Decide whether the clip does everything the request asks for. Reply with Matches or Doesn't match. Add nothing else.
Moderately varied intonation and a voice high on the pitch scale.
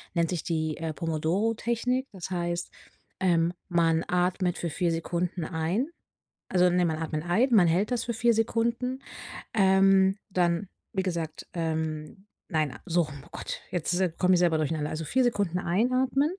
Doesn't match